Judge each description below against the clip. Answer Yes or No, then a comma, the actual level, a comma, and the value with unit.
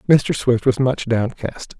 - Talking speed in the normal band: Yes, average, 165 wpm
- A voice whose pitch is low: Yes, low, 125 Hz